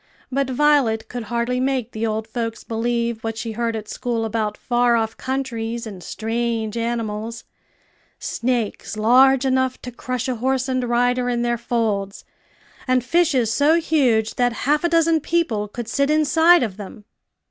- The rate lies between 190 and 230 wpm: No, average, 160 wpm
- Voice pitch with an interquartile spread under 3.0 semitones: Yes, narrow, 2.6 semitones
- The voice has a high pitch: Yes, high, 240 Hz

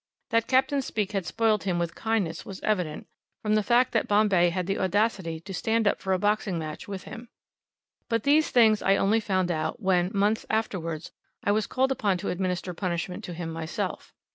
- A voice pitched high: Yes, high, 195 Hz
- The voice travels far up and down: No, average, 3.8 semitones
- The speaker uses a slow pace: No, average, 195 wpm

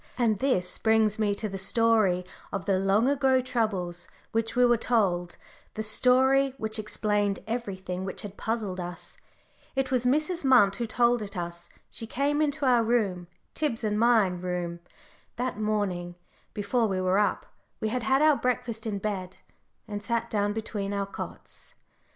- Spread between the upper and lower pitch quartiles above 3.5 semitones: Yes, average, 3.9 semitones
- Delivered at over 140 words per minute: Yes, average, 165 wpm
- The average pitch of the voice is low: No, high, 215 Hz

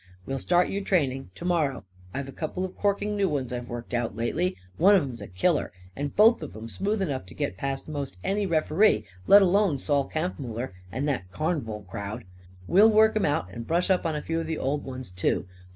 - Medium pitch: Yes, medium, 145 Hz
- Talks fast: Yes, fast, 215 wpm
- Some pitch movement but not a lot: No, wide, 7.2 semitones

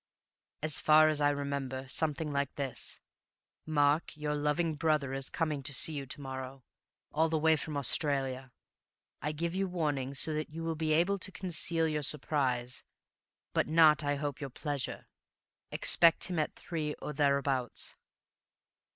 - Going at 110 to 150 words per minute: No, average, 160 wpm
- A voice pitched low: No, medium, 150 Hz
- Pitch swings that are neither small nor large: No, narrow, 2.3 semitones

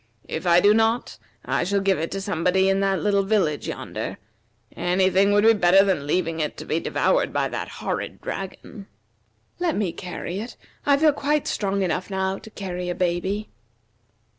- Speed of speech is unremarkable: Yes, average, 185 wpm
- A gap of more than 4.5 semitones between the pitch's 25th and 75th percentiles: No, narrow, 2.4 semitones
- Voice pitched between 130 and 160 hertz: No, high, 195 Hz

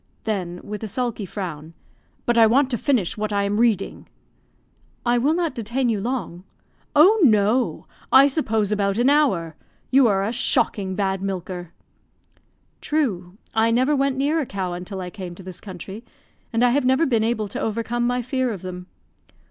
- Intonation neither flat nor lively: Yes, average, 4.8 semitones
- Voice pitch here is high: Yes, high, 220 Hz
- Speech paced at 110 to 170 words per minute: No, average, 180 wpm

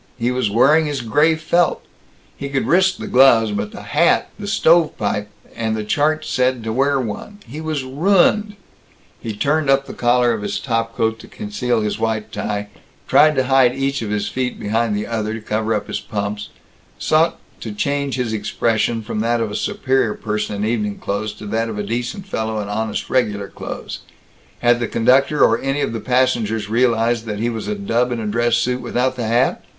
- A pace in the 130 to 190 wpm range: No, fast, 205 wpm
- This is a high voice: No, low, 120 Hz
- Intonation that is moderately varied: Yes, average, 4.0 semitones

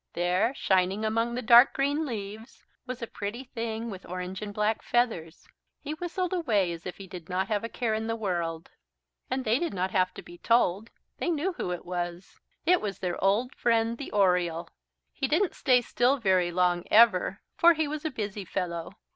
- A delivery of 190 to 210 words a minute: Yes, average, 195 wpm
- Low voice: No, high, 215 Hz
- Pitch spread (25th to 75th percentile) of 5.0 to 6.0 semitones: Yes, average, 5.3 semitones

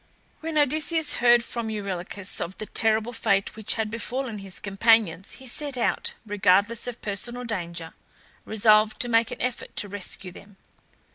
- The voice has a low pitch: No, high, 220 Hz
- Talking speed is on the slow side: No, average, 155 wpm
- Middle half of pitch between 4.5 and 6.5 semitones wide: No, average, 3.3 semitones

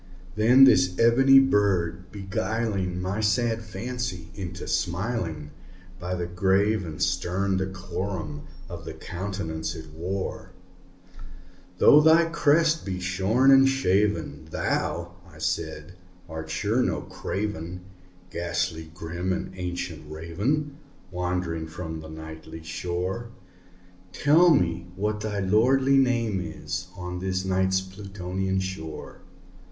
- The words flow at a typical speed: No, slow, 115 wpm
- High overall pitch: No, very low, 95 Hz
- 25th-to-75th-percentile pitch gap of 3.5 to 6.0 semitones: Yes, average, 4.0 semitones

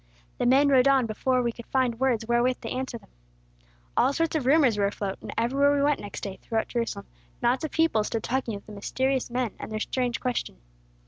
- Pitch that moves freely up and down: No, average, 3.0 semitones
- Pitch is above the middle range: Yes, high, 245 Hz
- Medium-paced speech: No, fast, 215 wpm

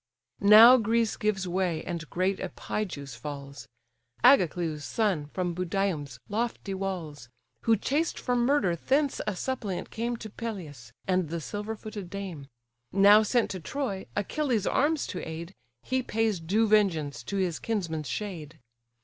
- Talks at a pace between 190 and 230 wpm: No, average, 140 wpm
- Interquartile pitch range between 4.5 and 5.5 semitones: Yes, average, 5.1 semitones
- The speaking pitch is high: Yes, high, 195 Hz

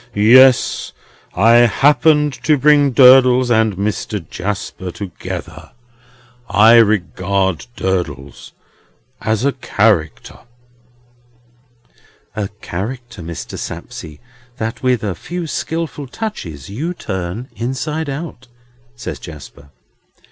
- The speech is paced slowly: Yes, slow, 95 wpm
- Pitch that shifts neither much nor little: No, wide, 5.9 semitones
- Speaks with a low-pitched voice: Yes, low, 115 Hz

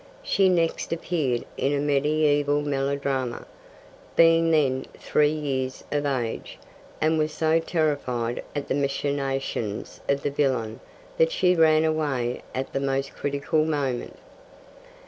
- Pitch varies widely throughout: No, narrow, 2.6 semitones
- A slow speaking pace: Yes, slow, 125 wpm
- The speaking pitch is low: No, medium, 145 Hz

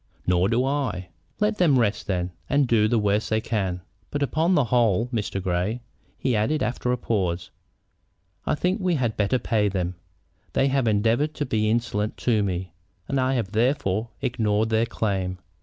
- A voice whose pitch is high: No, low, 115 Hz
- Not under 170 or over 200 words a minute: Yes, average, 175 wpm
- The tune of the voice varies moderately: Yes, average, 4.4 semitones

